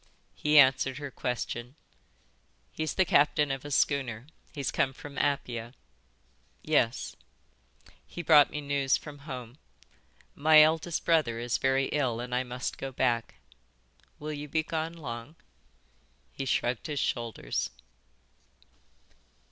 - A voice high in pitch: No, low, 135 Hz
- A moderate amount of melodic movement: Yes, average, 3.3 semitones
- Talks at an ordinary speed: No, slow, 125 wpm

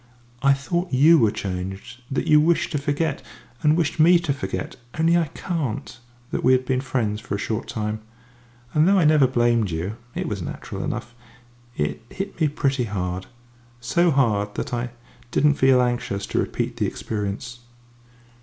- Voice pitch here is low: Yes, low, 130 Hz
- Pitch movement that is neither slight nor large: No, wide, 6.2 semitones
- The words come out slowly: No, average, 175 wpm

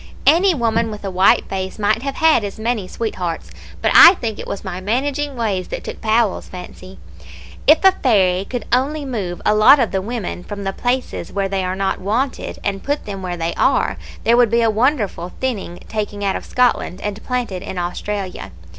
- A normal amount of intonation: Yes, average, 4.4 semitones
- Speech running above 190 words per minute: Yes, average, 200 wpm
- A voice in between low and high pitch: No, high, 210 Hz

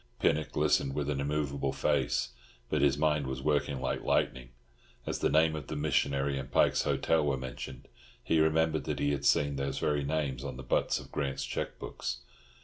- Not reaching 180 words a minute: No, average, 190 wpm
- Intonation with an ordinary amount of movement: No, narrow, 1.9 semitones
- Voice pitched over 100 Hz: No, very low, 70 Hz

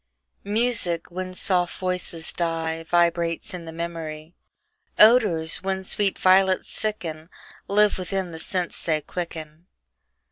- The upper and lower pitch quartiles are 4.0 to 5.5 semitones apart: No, narrow, 2.6 semitones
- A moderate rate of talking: No, slow, 115 wpm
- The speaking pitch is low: No, medium, 175 Hz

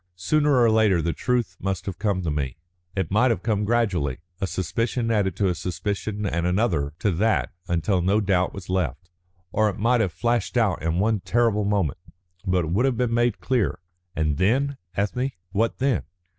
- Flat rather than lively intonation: No, average, 4.4 semitones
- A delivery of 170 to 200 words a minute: Yes, average, 190 wpm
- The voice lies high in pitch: No, low, 100 Hz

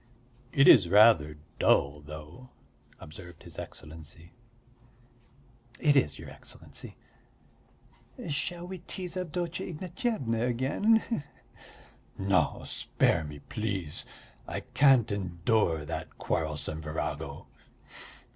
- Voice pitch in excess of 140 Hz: No, low, 105 Hz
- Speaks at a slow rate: Yes, slow, 100 wpm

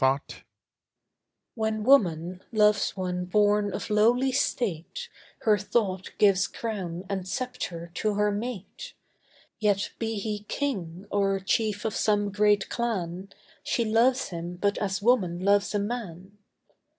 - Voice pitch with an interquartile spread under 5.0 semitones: Yes, average, 3.1 semitones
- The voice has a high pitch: Yes, high, 205 Hz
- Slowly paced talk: Yes, slow, 130 wpm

